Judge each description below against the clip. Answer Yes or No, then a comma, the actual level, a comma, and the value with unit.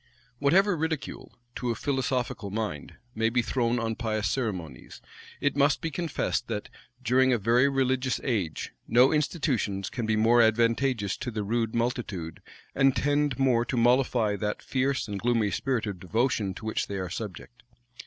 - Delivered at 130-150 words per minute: No, average, 165 wpm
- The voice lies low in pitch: Yes, low, 120 Hz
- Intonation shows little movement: No, average, 3.6 semitones